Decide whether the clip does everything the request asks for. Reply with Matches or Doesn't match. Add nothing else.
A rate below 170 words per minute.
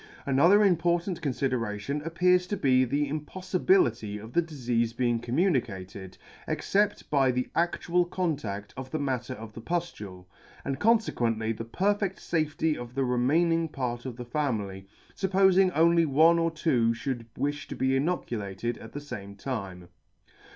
Matches